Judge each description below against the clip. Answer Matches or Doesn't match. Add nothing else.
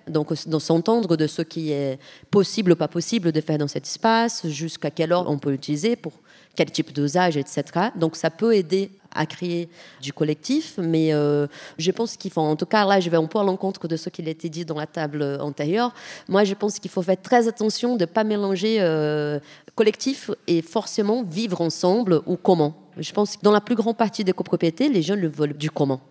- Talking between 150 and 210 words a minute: Doesn't match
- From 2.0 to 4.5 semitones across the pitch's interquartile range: Doesn't match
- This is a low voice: Doesn't match